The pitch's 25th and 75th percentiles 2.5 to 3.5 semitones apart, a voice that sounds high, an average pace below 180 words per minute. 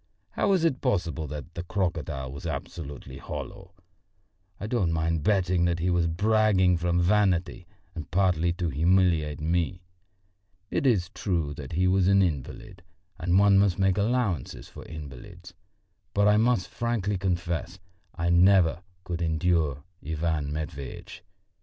No: average, 3.1 semitones; very low, 85 Hz; average, 140 wpm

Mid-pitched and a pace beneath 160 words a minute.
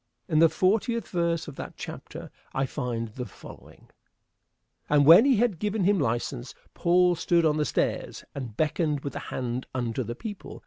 No: medium, 155 Hz; average, 175 wpm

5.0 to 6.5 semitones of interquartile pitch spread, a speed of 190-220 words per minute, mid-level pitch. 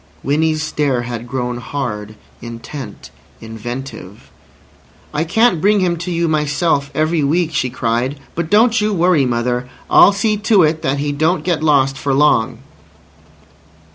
No: wide, 5.4 semitones; average, 145 wpm; medium, 145 Hz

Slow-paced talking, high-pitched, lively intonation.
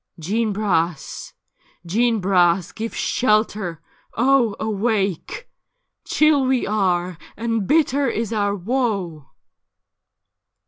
No: slow, 100 wpm; high, 215 Hz; average, 4.4 semitones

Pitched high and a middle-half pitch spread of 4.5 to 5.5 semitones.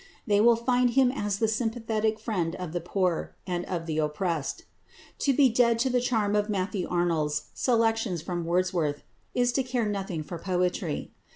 Yes: high, 200 Hz; average, 5.0 semitones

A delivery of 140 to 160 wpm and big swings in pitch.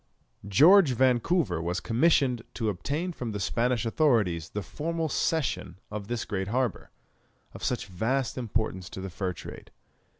Yes: average, 145 wpm; wide, 6.1 semitones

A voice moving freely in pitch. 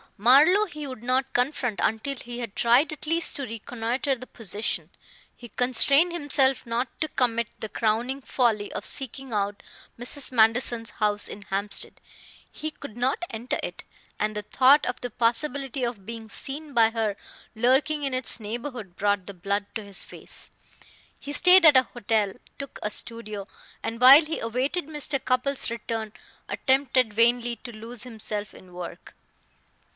No: average, 3.7 semitones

